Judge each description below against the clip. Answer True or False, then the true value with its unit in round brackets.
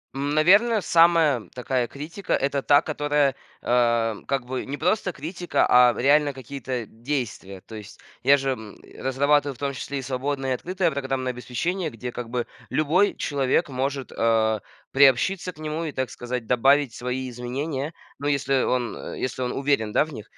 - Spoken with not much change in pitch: False (3.1 semitones)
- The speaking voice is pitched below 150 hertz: True (135 Hz)